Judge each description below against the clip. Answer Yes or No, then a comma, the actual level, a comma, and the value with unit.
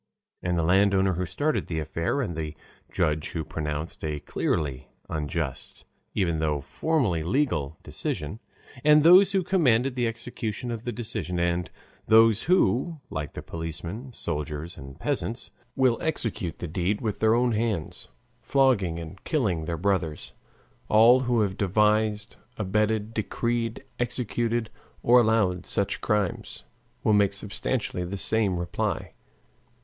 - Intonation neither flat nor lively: No, wide, 5.9 semitones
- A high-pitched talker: No, low, 105 Hz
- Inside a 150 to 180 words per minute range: No, slow, 135 wpm